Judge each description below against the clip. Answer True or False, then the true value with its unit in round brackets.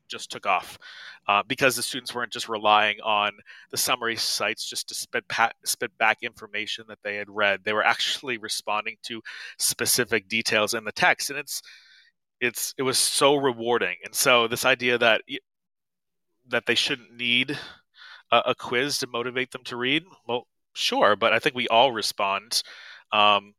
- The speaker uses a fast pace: False (175 wpm)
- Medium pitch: False (120 Hz)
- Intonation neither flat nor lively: True (3.5 semitones)